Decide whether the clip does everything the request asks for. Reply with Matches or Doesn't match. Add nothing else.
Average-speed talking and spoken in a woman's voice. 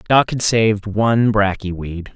Doesn't match